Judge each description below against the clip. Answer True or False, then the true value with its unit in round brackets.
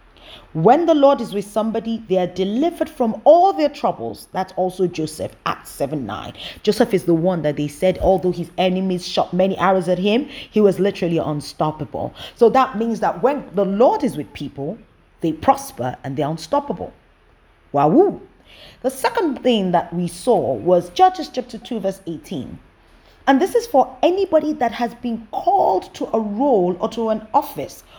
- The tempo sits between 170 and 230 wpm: True (180 wpm)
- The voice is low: False (215 Hz)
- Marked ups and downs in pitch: True (6.5 semitones)